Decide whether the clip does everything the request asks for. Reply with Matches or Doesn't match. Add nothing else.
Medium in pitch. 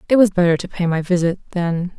Matches